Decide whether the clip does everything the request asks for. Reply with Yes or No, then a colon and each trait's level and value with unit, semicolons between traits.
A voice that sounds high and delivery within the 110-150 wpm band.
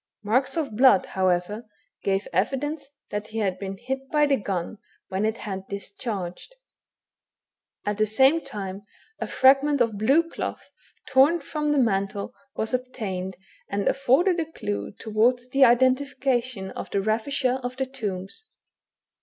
Yes: high, 235 Hz; average, 145 wpm